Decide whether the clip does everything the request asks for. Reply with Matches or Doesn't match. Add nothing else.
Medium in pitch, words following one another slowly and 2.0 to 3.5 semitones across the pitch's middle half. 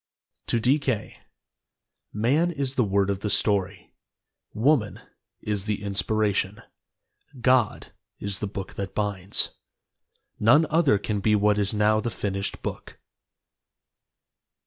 Doesn't match